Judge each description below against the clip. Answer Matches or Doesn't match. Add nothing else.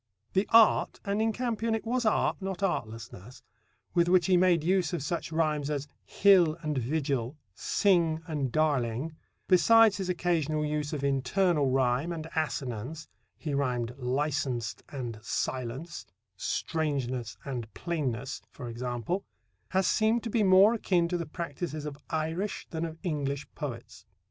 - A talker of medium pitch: Matches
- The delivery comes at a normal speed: Matches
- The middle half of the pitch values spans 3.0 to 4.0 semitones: Doesn't match